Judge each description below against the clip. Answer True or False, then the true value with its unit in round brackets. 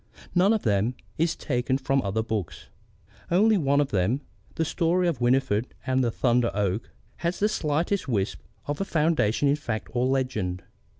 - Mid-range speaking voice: False (130 Hz)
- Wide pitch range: True (6.4 semitones)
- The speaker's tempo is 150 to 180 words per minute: True (170 wpm)